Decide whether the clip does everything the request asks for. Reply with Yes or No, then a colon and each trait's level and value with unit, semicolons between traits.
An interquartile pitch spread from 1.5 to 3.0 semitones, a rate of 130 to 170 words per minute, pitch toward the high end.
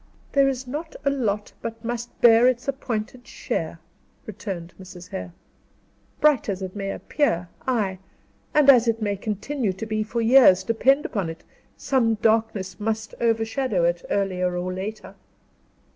No: average, 4.5 semitones; average, 150 wpm; high, 220 Hz